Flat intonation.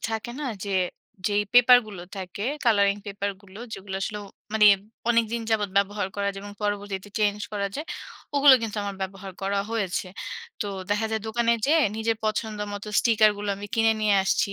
Yes: narrow, 1.8 semitones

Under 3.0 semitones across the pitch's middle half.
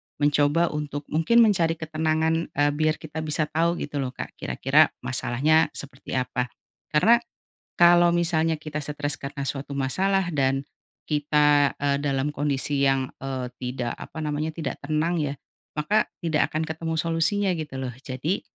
Yes: narrow, 2.6 semitones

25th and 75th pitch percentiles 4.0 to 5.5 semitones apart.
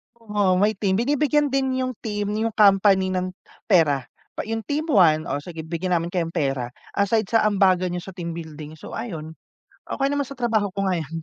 Yes: average, 5.2 semitones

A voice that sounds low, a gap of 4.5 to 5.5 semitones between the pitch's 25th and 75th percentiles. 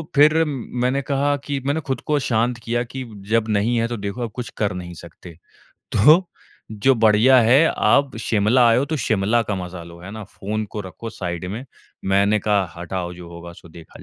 Yes: low, 110 Hz; average, 5.1 semitones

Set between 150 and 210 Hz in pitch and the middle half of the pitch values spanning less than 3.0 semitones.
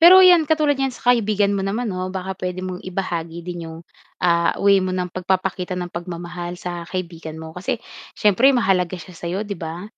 Yes: medium, 185 Hz; narrow, 2.6 semitones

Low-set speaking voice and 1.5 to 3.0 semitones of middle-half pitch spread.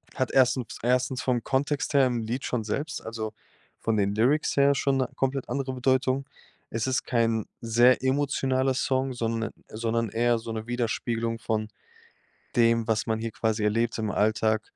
Yes: low, 120 Hz; average, 2.7 semitones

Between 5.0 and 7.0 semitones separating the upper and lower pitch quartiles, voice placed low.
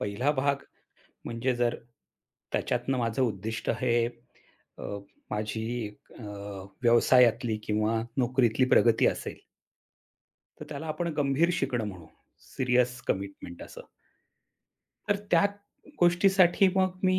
Yes: average, 5.3 semitones; low, 125 Hz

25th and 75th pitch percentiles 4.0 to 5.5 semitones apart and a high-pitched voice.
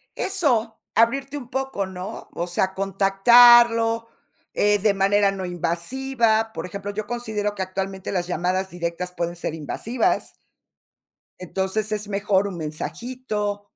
No: average, 3.5 semitones; high, 205 Hz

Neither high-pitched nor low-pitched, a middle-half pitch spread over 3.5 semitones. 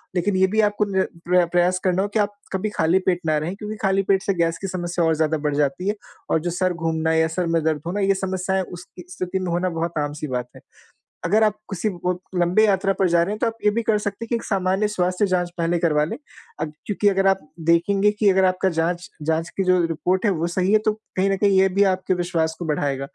No: medium, 180 Hz; average, 2.9 semitones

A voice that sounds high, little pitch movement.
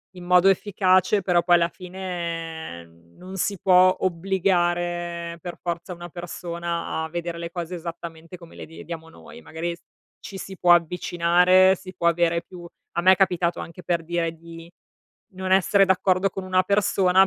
No: medium, 175 Hz; narrow, 1.6 semitones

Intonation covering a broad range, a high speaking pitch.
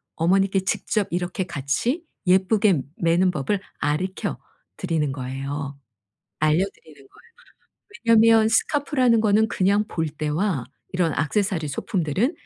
No: wide, 5.7 semitones; medium, 180 Hz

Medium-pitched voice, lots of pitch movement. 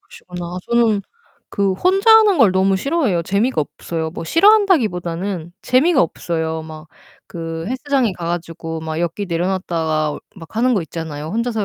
Yes: medium, 180 Hz; wide, 6.4 semitones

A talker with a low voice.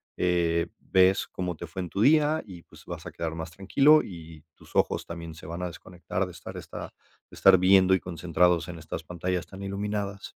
Yes: very low, 90 Hz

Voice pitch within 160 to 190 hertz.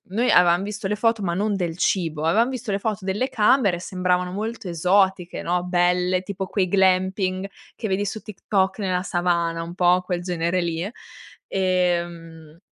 Yes: medium, 185 Hz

